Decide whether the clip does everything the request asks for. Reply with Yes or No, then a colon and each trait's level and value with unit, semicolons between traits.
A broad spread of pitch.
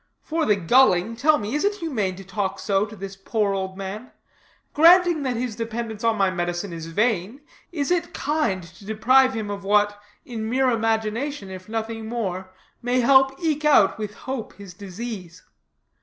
No: average, 4.8 semitones